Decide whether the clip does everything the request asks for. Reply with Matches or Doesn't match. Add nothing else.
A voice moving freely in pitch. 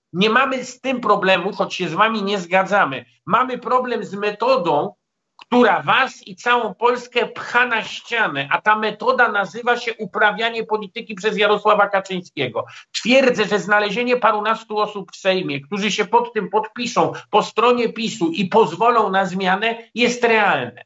Doesn't match